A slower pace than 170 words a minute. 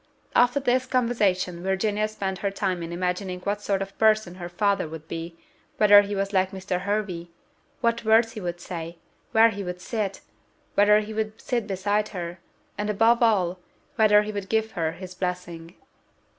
No: average, 175 wpm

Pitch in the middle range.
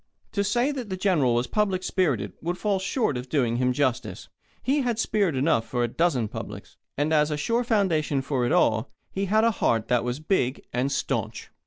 Yes: medium, 155 Hz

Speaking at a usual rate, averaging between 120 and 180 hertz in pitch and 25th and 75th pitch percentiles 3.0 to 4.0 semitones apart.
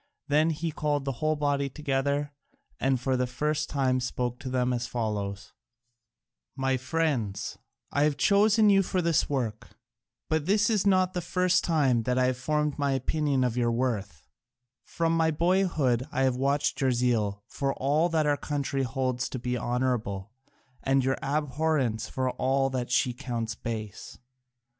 Yes: average, 165 wpm; low, 135 Hz; average, 3.7 semitones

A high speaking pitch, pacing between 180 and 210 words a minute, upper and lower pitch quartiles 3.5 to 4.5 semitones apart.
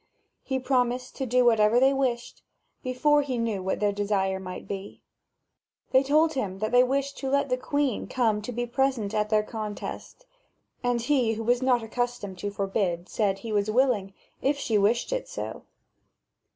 Yes: high, 240 Hz; average, 185 wpm; average, 4.0 semitones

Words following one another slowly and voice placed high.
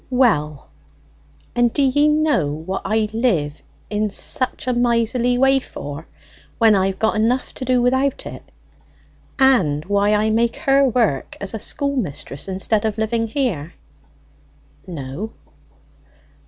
Yes: slow, 130 wpm; high, 225 Hz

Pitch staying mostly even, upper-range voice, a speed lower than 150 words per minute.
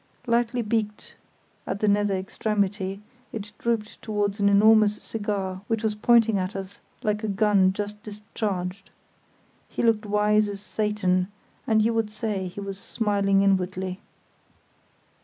Yes: narrow, 1.6 semitones; high, 210 Hz; average, 140 wpm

